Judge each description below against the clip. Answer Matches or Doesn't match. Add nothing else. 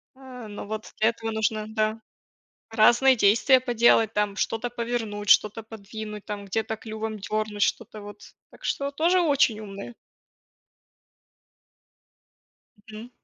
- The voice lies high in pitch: Matches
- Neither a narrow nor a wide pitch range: Doesn't match